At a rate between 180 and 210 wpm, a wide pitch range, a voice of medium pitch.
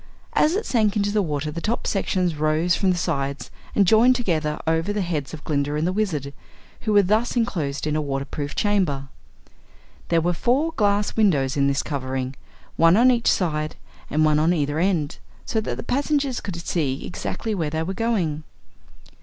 Yes: average, 190 wpm; wide, 5.8 semitones; medium, 170 Hz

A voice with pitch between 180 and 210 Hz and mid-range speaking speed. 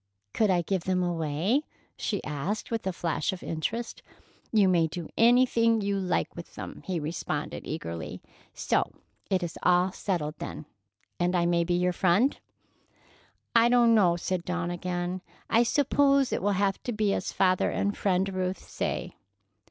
Yes: medium, 185 Hz; average, 165 wpm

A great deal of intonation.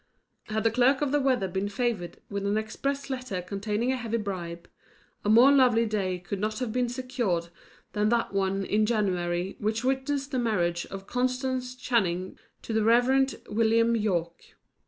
No: average, 4.4 semitones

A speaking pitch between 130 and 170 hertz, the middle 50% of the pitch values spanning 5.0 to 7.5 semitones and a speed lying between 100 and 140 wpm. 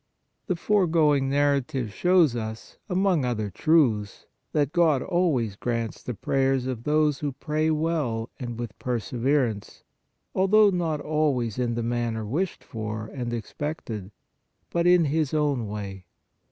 Yes: low, 135 Hz; average, 5.3 semitones; slow, 135 wpm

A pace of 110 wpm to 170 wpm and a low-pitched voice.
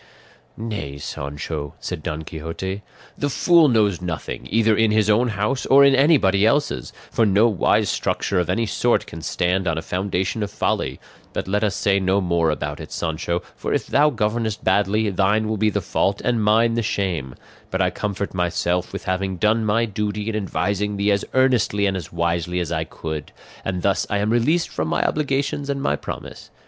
No: average, 195 wpm; low, 100 Hz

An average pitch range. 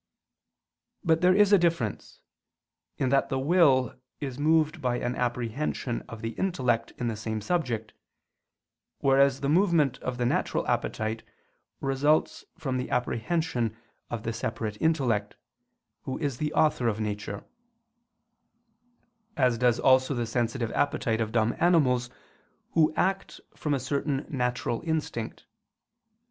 Yes: average, 4.7 semitones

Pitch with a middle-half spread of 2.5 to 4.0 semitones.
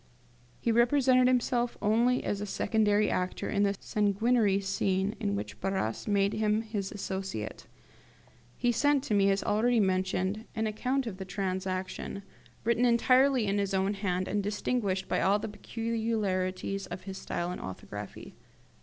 Yes: average, 3.2 semitones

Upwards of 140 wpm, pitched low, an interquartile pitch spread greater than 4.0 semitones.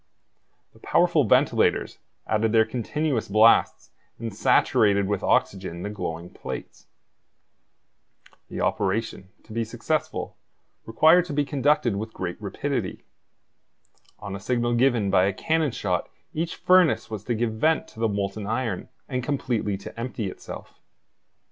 No: slow, 135 wpm; low, 110 Hz; average, 4.4 semitones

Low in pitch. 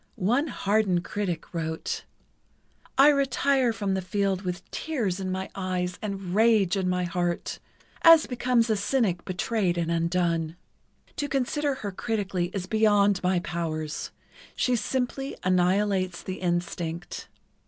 No: high, 190 Hz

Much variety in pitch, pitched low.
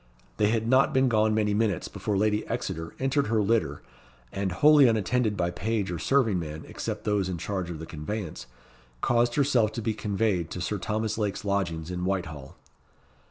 No: average, 4.1 semitones; low, 105 Hz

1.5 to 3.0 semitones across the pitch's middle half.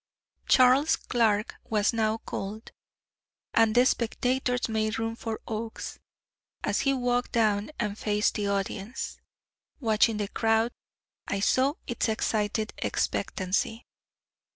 Yes: narrow, 2.5 semitones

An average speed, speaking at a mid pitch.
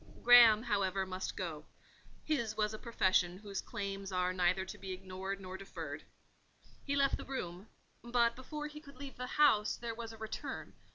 No: average, 175 wpm; high, 210 Hz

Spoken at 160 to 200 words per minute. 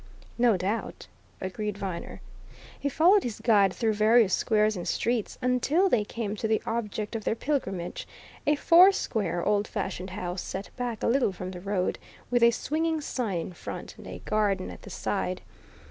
Yes: average, 175 wpm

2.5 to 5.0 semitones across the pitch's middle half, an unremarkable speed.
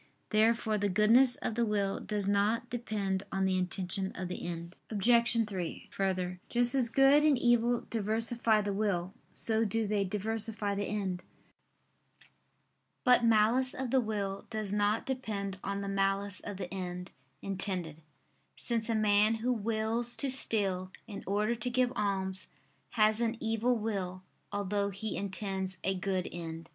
Yes: average, 2.9 semitones; average, 155 wpm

